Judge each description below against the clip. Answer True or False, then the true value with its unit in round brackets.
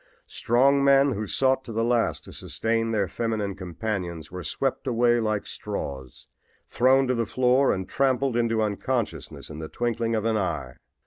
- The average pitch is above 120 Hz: False (115 Hz)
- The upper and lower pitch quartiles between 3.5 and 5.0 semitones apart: True (4.1 semitones)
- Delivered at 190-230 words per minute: False (170 wpm)